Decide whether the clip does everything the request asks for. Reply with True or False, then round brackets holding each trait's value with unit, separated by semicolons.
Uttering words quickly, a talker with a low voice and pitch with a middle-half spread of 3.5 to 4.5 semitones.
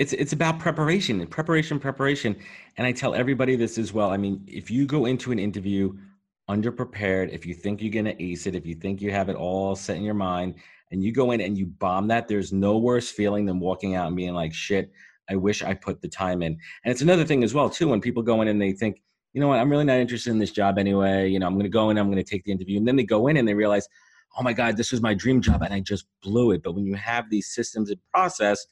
True (275 wpm; 105 Hz; 3.9 semitones)